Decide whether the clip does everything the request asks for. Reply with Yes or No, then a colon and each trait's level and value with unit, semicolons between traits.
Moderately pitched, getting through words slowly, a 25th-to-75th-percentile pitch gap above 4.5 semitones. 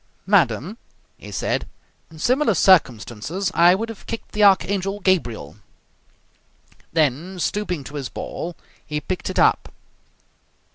Yes: medium, 180 Hz; slow, 125 wpm; average, 5.0 semitones